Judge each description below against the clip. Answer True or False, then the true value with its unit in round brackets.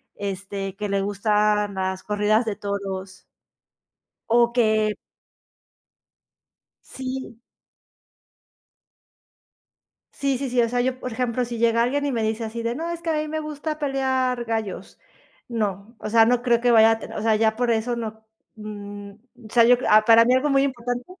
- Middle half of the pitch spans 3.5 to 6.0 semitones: False (3.1 semitones)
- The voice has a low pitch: False (230 Hz)